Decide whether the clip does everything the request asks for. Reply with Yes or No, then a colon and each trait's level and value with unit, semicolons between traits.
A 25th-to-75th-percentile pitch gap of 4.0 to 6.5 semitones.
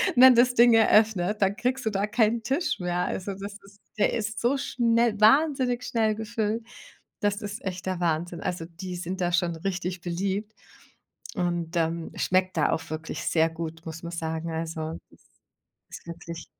Yes: average, 4.6 semitones